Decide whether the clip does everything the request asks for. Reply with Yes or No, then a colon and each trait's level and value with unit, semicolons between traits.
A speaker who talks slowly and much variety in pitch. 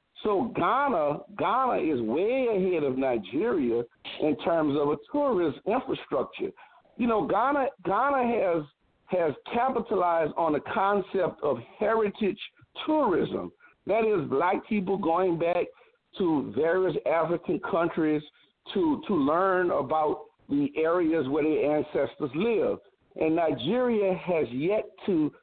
Yes: slow, 125 wpm; wide, 7.3 semitones